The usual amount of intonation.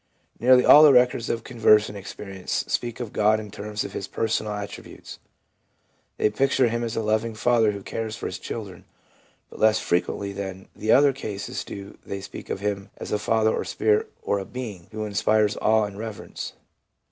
No: narrow, 2.0 semitones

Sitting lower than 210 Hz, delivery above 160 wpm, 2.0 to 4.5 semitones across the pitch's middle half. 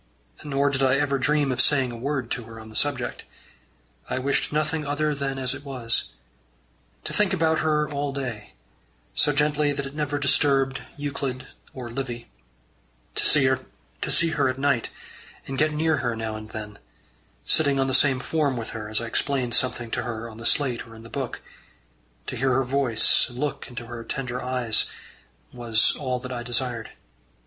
Yes: low, 135 Hz; average, 185 wpm; average, 3.1 semitones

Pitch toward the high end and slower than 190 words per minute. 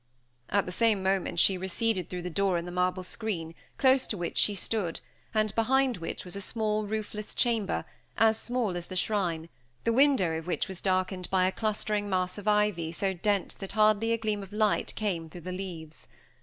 No: high, 195 Hz; average, 200 wpm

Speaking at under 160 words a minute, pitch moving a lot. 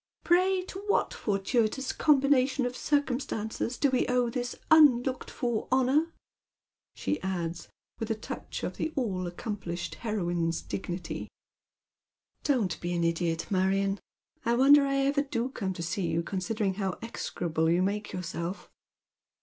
Yes: average, 145 wpm; wide, 6.5 semitones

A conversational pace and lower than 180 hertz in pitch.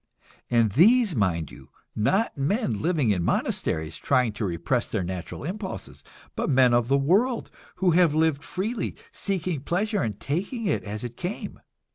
Yes: average, 160 wpm; medium, 140 Hz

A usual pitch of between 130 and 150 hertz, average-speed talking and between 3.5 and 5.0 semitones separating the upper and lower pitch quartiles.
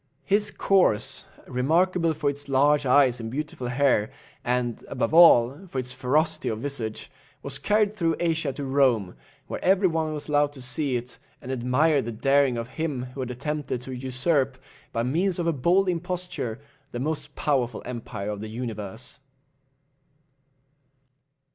Yes: medium, 140 Hz; average, 155 wpm; average, 4.4 semitones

